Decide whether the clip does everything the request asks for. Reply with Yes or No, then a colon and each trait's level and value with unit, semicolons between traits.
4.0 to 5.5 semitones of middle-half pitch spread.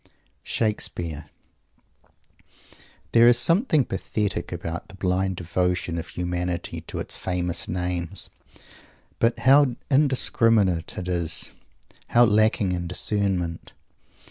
Yes: average, 4.6 semitones